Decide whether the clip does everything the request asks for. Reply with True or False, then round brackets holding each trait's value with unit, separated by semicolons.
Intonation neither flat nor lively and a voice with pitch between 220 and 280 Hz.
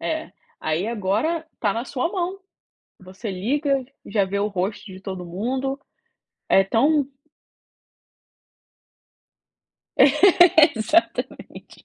False (7.4 semitones; 230 Hz)